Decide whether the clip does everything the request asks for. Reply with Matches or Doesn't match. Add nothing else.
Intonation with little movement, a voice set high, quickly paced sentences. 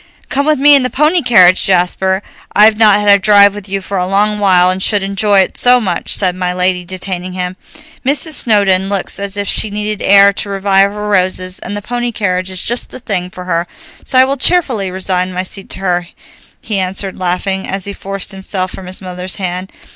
Matches